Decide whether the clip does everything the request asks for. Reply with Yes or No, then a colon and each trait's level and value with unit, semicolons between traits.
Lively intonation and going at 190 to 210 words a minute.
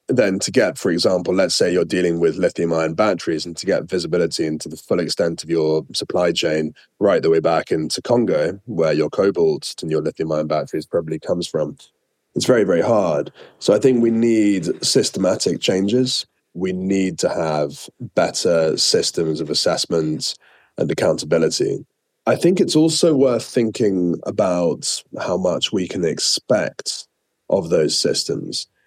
No: wide, 8.6 semitones; average, 160 wpm